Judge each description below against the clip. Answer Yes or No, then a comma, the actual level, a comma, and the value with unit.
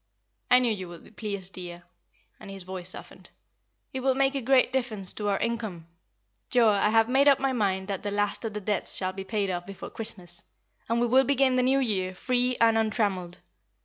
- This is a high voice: Yes, high, 215 Hz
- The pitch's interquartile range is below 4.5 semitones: No, average, 4.8 semitones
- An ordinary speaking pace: No, fast, 210 wpm